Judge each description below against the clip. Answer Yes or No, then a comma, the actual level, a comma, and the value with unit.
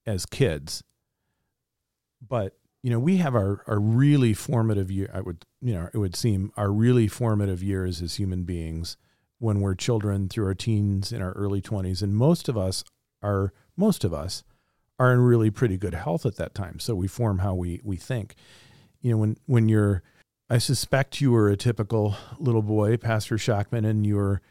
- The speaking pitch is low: Yes, low, 105 Hz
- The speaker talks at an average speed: Yes, average, 190 wpm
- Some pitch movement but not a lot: Yes, average, 3.7 semitones